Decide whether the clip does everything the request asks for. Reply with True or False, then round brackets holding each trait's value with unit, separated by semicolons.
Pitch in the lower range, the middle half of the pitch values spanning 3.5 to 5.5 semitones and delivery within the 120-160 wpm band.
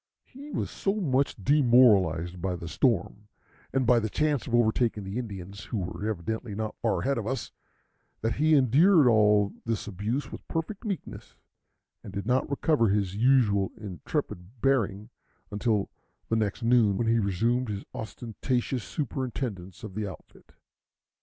True (115 Hz; 4.4 semitones; 155 wpm)